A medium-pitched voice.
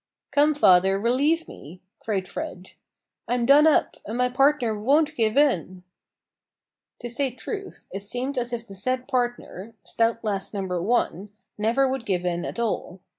No: high, 235 Hz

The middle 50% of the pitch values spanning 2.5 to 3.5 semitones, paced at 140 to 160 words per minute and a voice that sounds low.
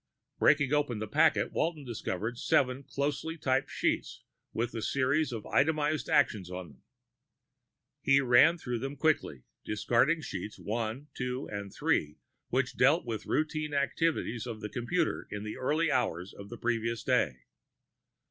No: average, 5.1 semitones; average, 150 wpm; low, 125 Hz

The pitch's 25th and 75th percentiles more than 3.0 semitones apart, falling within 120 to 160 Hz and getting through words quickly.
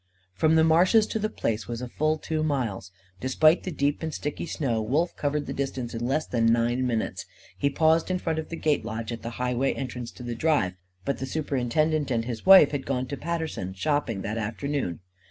Yes: average, 5.0 semitones; low, 135 Hz; fast, 210 wpm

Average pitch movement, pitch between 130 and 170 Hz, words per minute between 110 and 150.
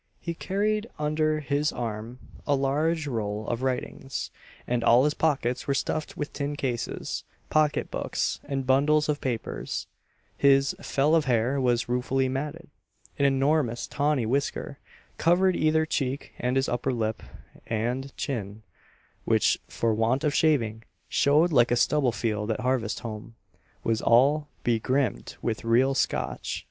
Yes: average, 3.9 semitones; low, 135 Hz; average, 145 wpm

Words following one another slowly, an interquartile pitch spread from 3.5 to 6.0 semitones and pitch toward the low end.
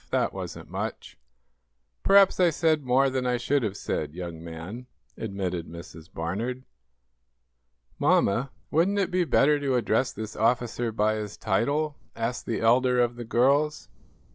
No: average, 145 wpm; average, 4.9 semitones; low, 120 Hz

